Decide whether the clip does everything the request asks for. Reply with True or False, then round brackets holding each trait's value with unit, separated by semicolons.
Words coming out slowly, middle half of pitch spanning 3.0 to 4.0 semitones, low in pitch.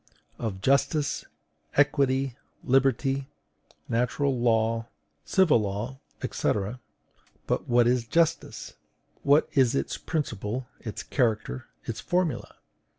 True (95 wpm; 3.5 semitones; 125 Hz)